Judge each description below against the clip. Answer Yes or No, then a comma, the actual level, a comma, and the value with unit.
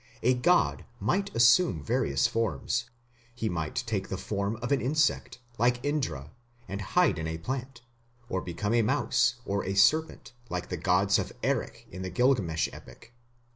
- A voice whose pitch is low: Yes, low, 115 Hz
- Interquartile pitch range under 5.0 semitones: No, wide, 5.6 semitones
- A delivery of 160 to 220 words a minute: Yes, average, 165 wpm